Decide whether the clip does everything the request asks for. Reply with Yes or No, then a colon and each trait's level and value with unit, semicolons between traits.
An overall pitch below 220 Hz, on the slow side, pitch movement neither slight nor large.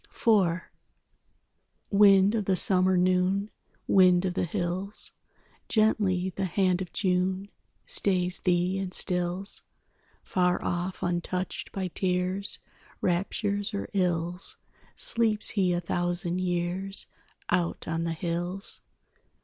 No: medium, 185 Hz; slow, 110 wpm; narrow, 1.8 semitones